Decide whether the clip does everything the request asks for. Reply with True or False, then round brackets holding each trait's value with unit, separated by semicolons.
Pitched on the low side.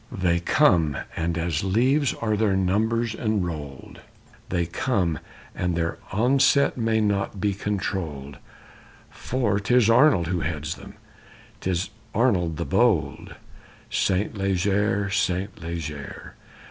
True (95 Hz)